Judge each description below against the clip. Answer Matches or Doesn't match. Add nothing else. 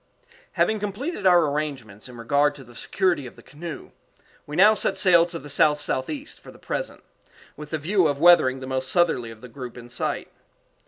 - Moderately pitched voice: Matches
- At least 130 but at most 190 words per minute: Doesn't match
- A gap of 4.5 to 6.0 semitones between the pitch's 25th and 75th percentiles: Matches